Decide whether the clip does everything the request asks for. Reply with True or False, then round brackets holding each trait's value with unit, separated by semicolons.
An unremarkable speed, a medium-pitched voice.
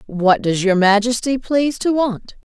False (165 wpm; 225 Hz)